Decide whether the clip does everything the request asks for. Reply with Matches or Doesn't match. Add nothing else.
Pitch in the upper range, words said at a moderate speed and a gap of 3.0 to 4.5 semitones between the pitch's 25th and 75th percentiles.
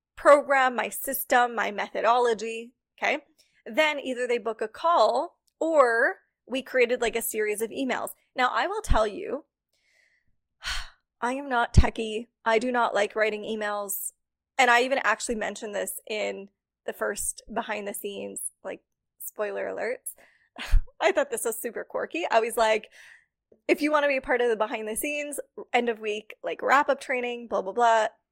Matches